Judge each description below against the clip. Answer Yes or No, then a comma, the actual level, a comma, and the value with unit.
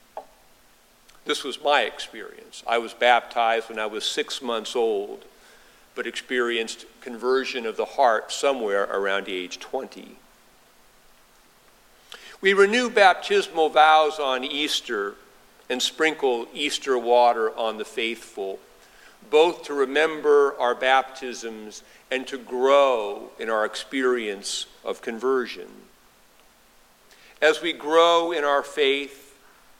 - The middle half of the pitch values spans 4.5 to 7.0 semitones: Yes, average, 4.9 semitones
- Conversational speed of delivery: No, slow, 110 wpm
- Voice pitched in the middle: No, low, 130 Hz